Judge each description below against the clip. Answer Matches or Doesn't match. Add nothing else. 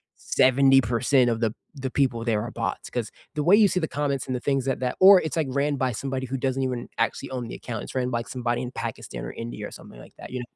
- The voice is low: Matches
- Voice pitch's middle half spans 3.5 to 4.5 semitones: Doesn't match